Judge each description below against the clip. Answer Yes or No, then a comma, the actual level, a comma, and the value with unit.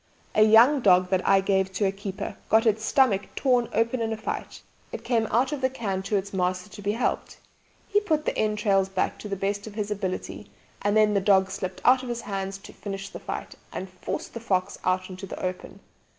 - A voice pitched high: Yes, high, 205 Hz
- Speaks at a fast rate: Yes, fast, 225 wpm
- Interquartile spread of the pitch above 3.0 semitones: No, average, 2.7 semitones